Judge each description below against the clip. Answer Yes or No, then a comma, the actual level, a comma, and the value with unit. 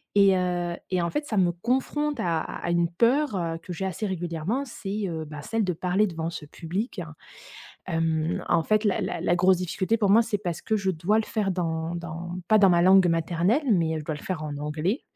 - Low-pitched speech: No, medium, 180 Hz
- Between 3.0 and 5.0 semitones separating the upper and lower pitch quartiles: Yes, average, 4.1 semitones